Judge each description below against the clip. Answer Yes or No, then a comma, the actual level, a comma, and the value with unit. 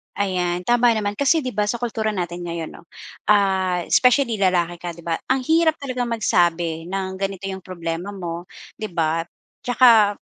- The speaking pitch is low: No, high, 190 Hz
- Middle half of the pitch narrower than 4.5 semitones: No, average, 4.9 semitones